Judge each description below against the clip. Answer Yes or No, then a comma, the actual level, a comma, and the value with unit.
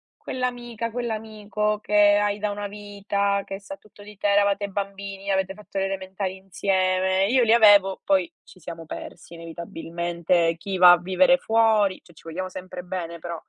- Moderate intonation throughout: No, narrow, 2.2 semitones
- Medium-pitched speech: No, high, 200 Hz